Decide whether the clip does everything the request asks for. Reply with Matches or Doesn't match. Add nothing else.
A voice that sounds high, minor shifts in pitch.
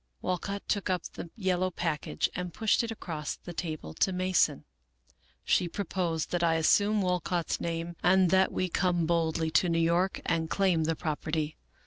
Doesn't match